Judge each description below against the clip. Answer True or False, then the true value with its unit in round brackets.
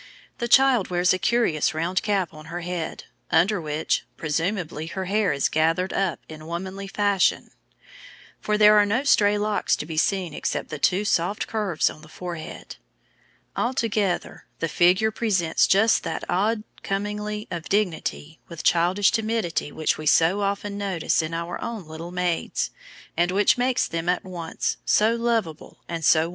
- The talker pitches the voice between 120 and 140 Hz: False (185 Hz)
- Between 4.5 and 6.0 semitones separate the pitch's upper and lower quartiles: False (4.1 semitones)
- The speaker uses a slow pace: False (165 wpm)